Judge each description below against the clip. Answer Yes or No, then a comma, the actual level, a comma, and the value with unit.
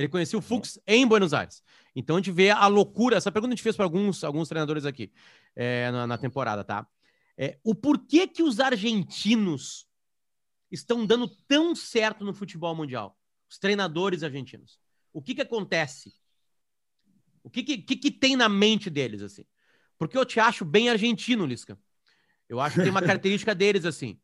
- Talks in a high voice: Yes, high, 195 Hz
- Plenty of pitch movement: Yes, wide, 7.4 semitones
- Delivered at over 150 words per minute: Yes, average, 180 wpm